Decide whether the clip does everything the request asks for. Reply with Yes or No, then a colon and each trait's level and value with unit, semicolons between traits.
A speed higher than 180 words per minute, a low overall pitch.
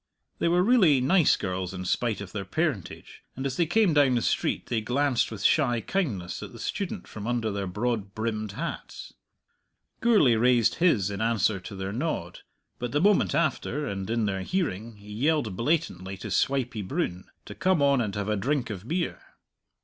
Yes: average, 190 wpm; low, 115 Hz